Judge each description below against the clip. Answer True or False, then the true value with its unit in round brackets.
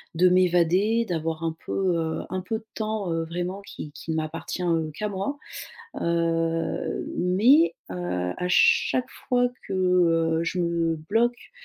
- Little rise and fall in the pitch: False (3.6 semitones)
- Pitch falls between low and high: True (175 Hz)